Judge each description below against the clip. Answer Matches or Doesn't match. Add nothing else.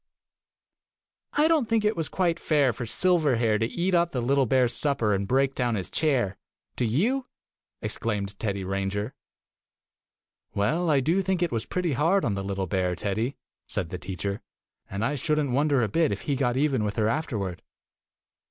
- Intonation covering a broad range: Matches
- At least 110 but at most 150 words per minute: Doesn't match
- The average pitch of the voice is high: Doesn't match